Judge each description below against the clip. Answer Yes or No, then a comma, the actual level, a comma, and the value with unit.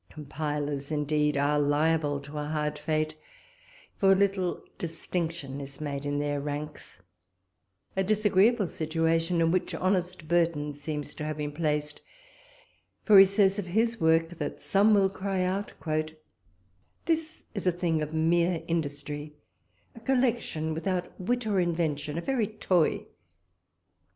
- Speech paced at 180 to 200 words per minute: No, slow, 135 wpm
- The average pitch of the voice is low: No, medium, 165 Hz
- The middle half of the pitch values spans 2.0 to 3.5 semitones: No, average, 4.3 semitones